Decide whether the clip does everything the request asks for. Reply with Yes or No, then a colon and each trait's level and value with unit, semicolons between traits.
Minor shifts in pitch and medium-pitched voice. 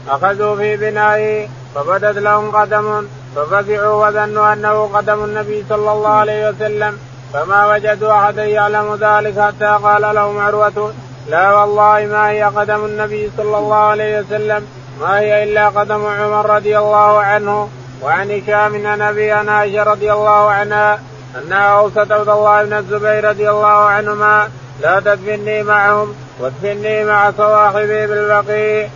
No: narrow, 0.5 semitones; high, 210 Hz